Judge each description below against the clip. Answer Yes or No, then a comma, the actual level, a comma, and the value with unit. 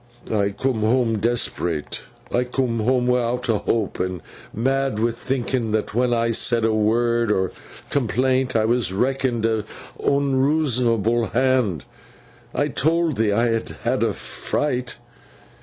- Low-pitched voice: Yes, low, 120 Hz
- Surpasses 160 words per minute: No, average, 140 wpm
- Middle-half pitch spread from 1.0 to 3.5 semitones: Yes, average, 2.8 semitones